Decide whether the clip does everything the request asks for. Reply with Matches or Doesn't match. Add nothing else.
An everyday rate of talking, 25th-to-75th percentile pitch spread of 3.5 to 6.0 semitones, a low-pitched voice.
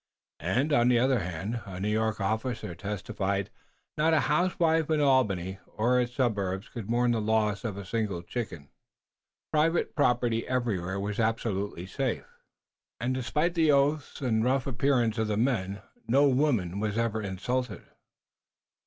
Matches